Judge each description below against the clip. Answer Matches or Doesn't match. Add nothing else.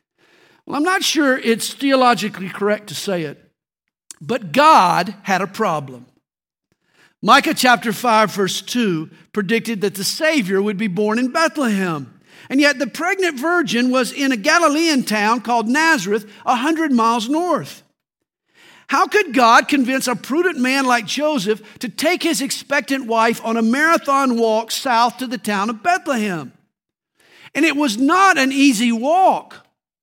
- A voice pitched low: Doesn't match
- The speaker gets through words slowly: Doesn't match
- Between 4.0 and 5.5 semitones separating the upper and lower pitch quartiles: Matches